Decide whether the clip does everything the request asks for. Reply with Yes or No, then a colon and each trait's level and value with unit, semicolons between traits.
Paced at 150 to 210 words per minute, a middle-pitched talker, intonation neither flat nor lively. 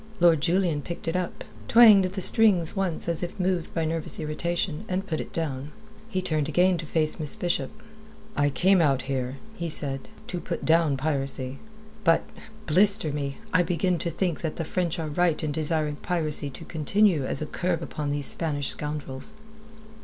Yes: average, 180 wpm; medium, 165 Hz; average, 3.3 semitones